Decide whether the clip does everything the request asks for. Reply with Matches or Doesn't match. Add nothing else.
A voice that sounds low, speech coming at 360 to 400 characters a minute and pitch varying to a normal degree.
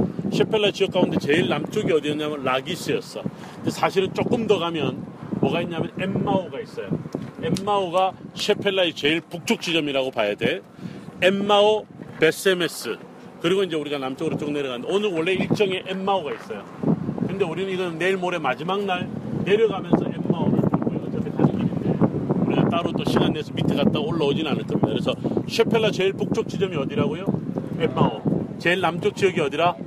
Doesn't match